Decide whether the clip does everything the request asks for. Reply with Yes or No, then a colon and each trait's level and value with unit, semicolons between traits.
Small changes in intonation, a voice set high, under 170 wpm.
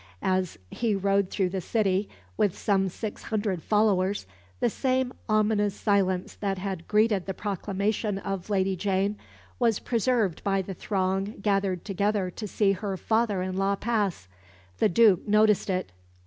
Yes: narrow, 2.0 semitones; high, 200 Hz; average, 150 wpm